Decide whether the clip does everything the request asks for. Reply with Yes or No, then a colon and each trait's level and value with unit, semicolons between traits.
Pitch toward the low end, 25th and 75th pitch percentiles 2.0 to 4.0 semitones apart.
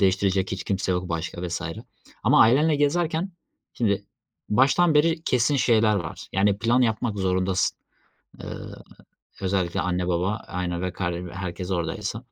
No: very low, 95 Hz; average, 5.1 semitones